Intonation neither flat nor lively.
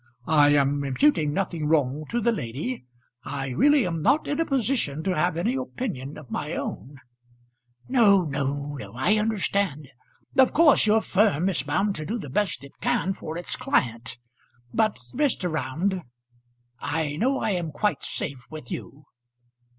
No: wide, 7.4 semitones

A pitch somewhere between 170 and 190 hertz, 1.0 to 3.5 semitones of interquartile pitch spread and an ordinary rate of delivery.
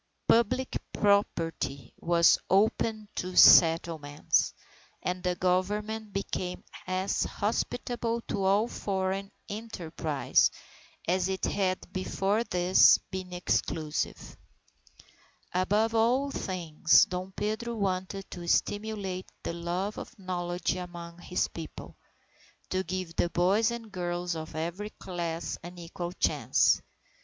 No: medium, 185 Hz; average, 3.0 semitones; slow, 110 wpm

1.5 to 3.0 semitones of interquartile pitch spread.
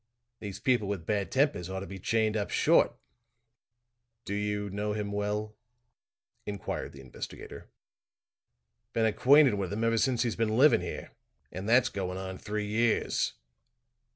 Yes: narrow, 2.6 semitones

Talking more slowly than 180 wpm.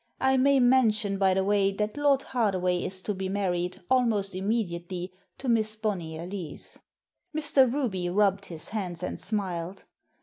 Yes: average, 155 wpm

